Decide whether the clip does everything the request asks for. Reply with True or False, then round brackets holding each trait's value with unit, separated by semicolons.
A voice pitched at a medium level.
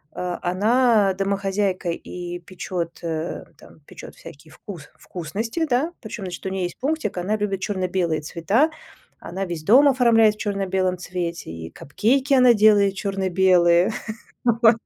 False (195 Hz)